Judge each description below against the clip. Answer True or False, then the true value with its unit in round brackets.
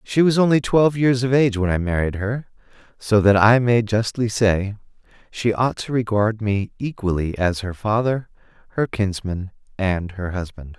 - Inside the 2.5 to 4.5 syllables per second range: False (4.7 syllables/s)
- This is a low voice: True (110 Hz)